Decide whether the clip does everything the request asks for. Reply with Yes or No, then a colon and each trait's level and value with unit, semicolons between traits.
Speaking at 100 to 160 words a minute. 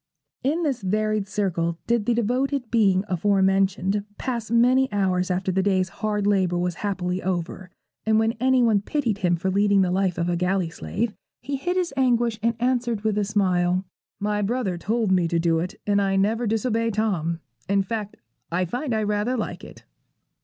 No: average, 185 wpm